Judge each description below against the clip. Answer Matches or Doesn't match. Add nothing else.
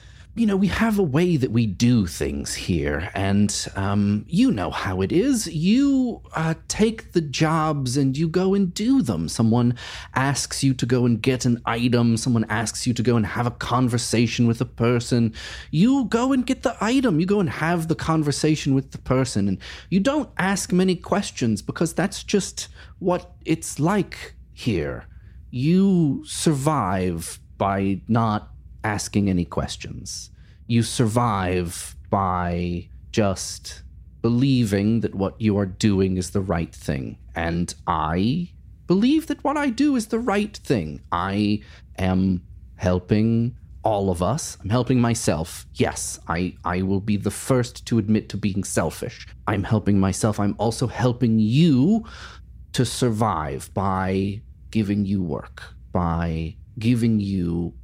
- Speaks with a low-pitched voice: Matches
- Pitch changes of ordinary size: Doesn't match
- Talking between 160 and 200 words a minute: Doesn't match